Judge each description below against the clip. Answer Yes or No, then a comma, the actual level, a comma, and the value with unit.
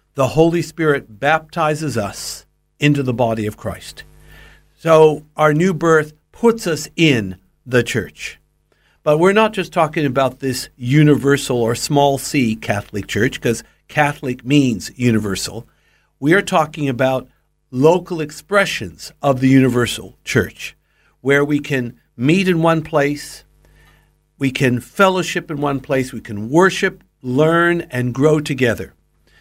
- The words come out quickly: No, slow, 135 wpm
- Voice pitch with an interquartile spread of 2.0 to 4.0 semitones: No, average, 4.4 semitones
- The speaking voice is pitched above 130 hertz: Yes, medium, 140 Hz